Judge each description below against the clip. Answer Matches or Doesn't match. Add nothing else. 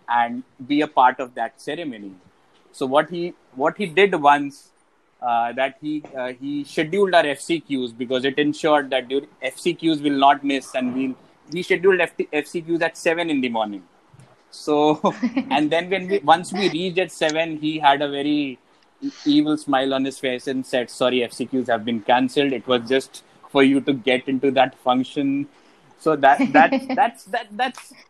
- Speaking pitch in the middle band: Matches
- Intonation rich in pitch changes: Doesn't match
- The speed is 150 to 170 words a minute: Doesn't match